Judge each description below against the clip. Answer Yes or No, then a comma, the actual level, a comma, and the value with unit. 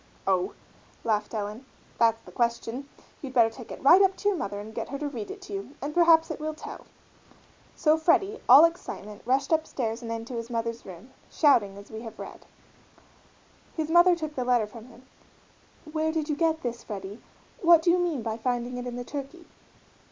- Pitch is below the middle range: No, very high, 255 Hz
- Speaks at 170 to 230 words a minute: Yes, average, 200 wpm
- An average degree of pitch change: No, wide, 5.8 semitones